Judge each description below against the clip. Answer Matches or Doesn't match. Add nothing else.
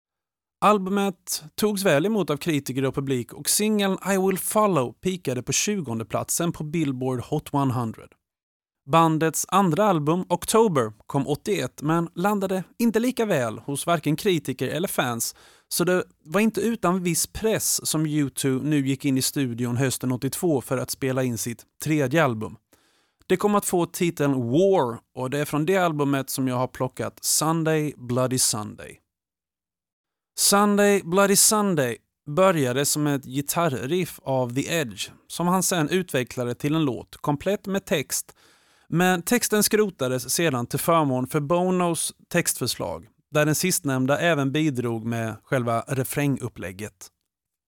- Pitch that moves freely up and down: Matches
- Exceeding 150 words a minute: Doesn't match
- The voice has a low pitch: Doesn't match